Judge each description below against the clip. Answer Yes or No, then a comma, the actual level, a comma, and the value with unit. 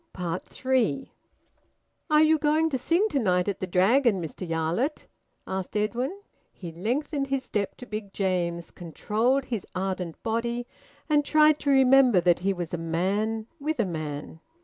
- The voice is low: No, high, 215 Hz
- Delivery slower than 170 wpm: Yes, average, 155 wpm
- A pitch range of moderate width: No, wide, 7.1 semitones